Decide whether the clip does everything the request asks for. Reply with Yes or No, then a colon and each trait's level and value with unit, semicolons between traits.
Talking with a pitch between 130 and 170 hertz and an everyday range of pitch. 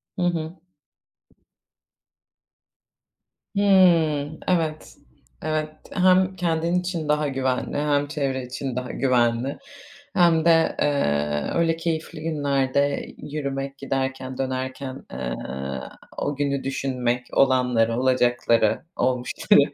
Yes: medium, 140 Hz; average, 3.6 semitones